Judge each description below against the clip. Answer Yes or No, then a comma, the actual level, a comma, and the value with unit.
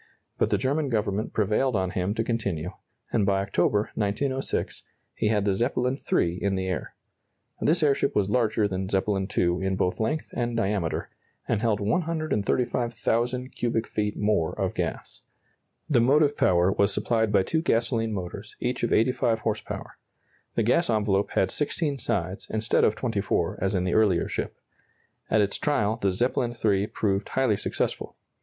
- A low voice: Yes, low, 110 Hz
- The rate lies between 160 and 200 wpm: Yes, average, 165 wpm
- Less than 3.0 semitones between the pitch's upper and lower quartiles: No, average, 3.7 semitones